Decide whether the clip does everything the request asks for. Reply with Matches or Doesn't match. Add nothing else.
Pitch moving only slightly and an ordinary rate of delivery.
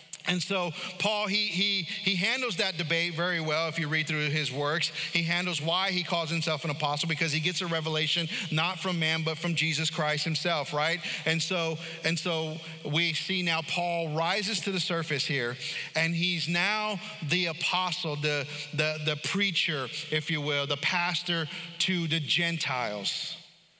Matches